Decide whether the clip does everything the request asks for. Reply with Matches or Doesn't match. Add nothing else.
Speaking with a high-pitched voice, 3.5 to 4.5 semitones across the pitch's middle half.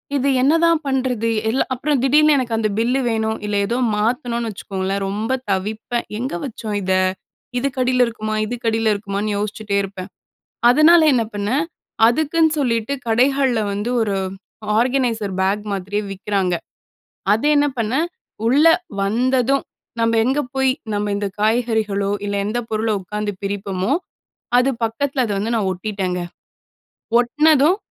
Matches